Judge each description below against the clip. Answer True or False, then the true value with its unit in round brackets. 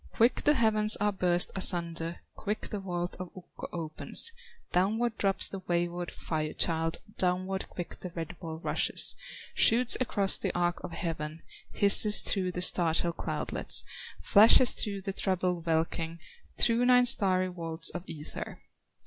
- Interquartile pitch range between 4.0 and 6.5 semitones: False (3.3 semitones)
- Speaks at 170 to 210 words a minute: False (145 wpm)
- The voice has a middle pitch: True (180 Hz)